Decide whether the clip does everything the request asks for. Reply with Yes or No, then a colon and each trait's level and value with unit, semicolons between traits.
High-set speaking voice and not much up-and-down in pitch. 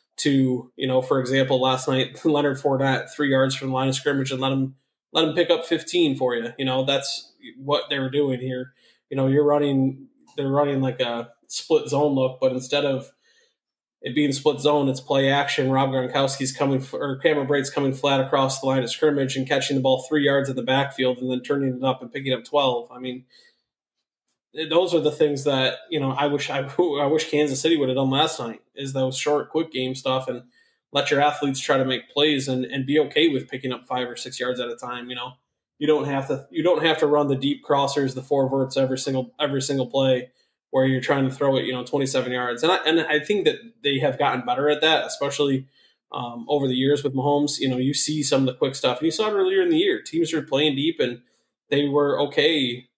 No: low, 135 Hz; narrow, 2.0 semitones